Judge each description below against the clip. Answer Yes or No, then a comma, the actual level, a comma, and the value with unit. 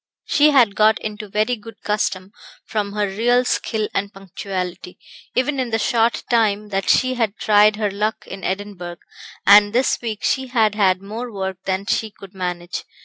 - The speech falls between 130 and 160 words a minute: No, average, 175 wpm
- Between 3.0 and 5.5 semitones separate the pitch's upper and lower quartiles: No, narrow, 2.6 semitones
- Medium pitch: No, high, 210 Hz